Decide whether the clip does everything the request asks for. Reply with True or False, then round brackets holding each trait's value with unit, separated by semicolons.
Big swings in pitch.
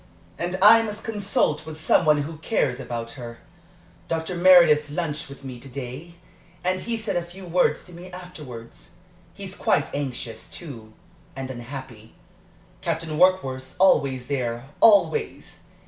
True (5.8 semitones)